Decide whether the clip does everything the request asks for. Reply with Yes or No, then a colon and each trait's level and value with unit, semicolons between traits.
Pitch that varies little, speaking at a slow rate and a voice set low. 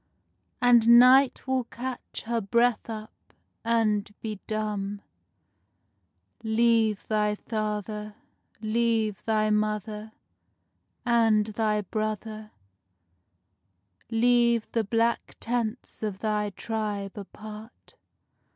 No: narrow, 1.6 semitones; slow, 85 wpm; high, 220 Hz